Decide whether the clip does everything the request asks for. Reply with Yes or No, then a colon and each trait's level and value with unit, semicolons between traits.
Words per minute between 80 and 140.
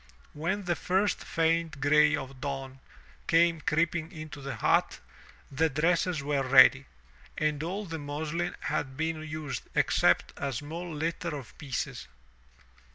Yes: slow, 135 wpm